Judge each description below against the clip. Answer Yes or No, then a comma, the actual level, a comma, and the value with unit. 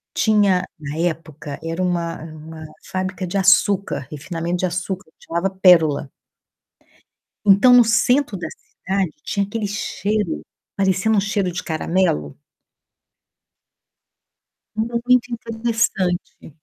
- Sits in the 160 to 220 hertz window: Yes, medium, 185 Hz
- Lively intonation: No, average, 4.0 semitones